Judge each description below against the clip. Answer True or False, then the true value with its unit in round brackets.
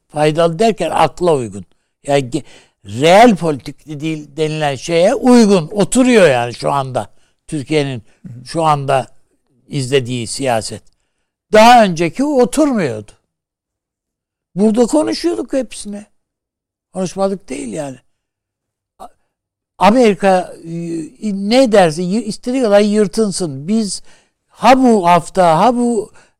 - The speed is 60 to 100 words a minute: True (95 wpm)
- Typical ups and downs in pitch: False (8.3 semitones)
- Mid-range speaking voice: True (165 Hz)